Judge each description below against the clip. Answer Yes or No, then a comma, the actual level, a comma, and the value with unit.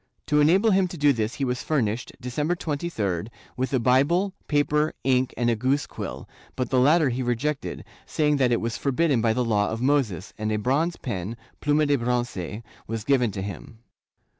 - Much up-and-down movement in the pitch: No, average, 4.4 semitones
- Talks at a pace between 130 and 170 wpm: No, average, 190 wpm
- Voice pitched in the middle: No, low, 130 Hz